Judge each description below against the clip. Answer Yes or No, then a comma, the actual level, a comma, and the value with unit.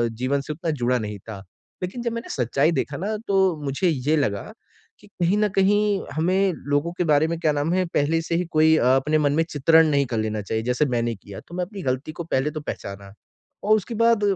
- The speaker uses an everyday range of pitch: No, wide, 5.8 semitones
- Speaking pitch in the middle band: Yes, medium, 155 Hz